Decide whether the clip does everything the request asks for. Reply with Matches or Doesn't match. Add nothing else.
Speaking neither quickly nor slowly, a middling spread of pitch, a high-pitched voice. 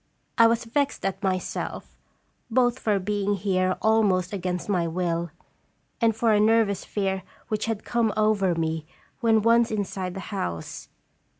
Matches